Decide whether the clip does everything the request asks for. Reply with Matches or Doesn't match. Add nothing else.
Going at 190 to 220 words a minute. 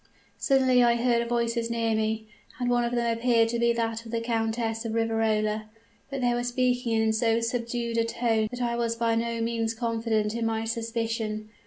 Matches